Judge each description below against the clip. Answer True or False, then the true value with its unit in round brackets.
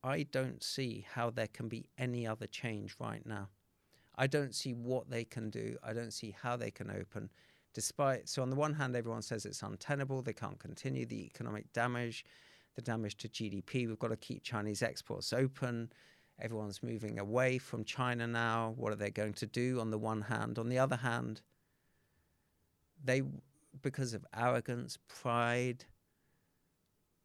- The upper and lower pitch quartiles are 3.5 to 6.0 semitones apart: False (2.9 semitones)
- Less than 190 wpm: True (170 wpm)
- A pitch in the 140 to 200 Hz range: False (115 Hz)